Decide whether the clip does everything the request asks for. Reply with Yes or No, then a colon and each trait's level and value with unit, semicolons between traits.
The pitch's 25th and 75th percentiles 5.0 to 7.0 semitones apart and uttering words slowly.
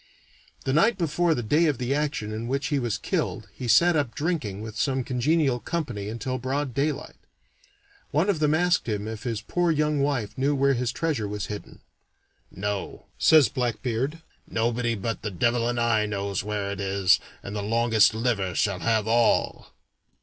No: average, 5.3 semitones; average, 180 wpm